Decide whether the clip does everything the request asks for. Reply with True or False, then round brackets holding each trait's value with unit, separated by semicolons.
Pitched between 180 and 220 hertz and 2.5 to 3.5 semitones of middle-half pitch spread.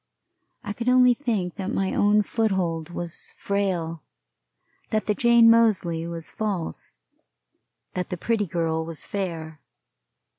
False (190 Hz; 4.6 semitones)